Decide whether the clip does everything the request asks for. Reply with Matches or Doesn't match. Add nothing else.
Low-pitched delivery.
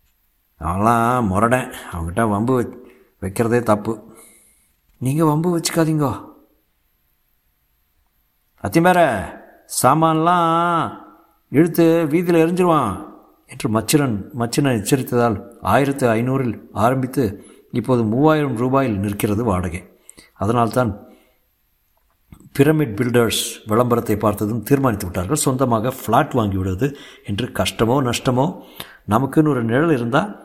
Matches